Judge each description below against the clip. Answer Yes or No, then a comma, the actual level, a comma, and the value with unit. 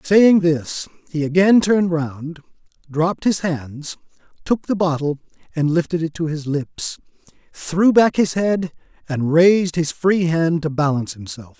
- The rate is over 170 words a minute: No, average, 155 wpm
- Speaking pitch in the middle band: Yes, medium, 165 Hz